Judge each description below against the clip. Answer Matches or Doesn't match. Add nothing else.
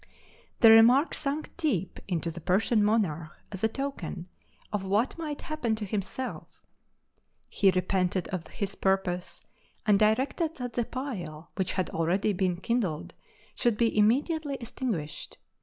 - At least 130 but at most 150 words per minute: Matches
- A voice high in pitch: Matches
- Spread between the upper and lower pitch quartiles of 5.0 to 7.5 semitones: Matches